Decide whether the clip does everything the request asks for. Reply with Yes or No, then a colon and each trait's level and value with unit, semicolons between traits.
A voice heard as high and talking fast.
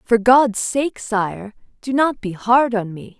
No: high, 230 Hz; average, 190 wpm